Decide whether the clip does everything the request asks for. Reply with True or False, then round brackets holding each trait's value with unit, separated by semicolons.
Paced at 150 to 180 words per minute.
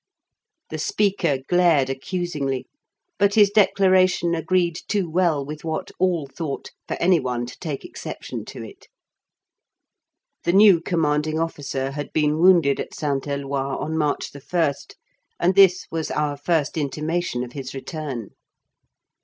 False (135 wpm)